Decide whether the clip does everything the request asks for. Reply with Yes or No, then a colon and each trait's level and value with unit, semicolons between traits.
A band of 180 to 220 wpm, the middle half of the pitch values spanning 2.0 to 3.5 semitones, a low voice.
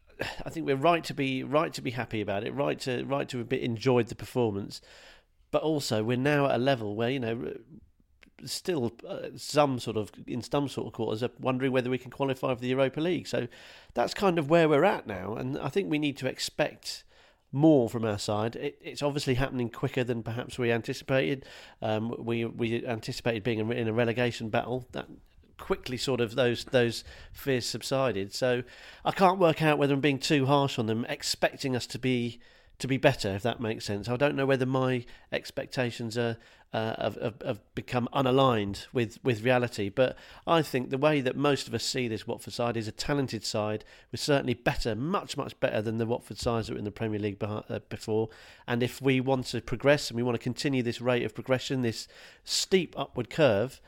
Yes: fast, 205 wpm; average, 3.0 semitones; low, 125 Hz